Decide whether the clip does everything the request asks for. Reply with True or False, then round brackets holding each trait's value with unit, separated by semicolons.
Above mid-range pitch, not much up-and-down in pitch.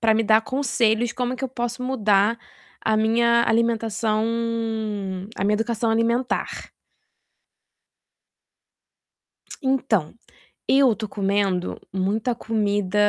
True (225 Hz; 2.2 semitones)